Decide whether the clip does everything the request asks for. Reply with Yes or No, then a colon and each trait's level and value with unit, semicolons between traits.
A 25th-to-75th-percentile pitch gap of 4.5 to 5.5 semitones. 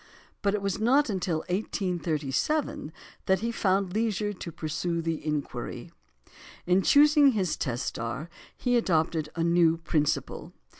Yes: average, 5.2 semitones